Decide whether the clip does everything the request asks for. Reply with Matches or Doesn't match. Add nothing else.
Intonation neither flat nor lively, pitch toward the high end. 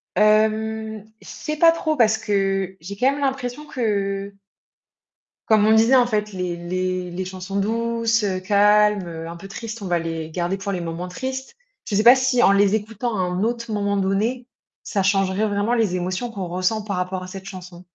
Matches